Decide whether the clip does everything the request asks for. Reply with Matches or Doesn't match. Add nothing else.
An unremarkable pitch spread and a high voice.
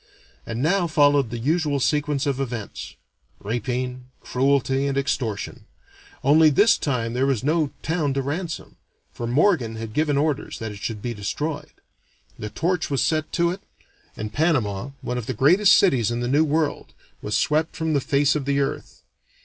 Doesn't match